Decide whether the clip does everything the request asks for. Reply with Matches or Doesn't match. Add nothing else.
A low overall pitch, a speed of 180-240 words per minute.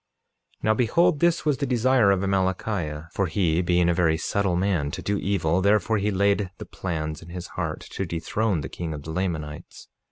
Matches